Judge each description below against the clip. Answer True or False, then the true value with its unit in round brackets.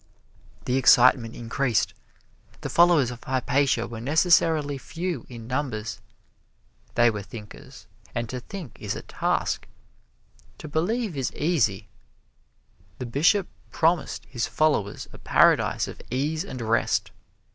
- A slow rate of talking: True (125 wpm)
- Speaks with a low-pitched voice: True (130 Hz)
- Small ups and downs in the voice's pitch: False (5.2 semitones)